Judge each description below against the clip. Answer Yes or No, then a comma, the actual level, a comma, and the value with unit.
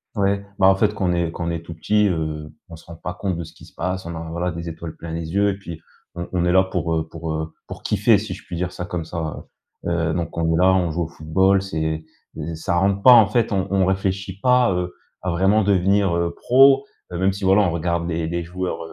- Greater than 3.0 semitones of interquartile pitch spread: No, average, 2.7 semitones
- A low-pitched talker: Yes, very low, 90 Hz